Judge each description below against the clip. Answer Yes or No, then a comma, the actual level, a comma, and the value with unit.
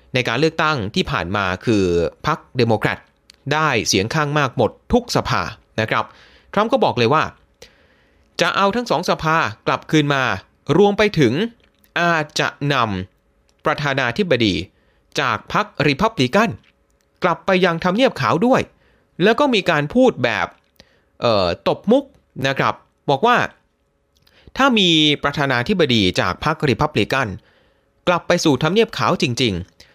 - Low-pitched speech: No, medium, 145 Hz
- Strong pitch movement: Yes, wide, 7.8 semitones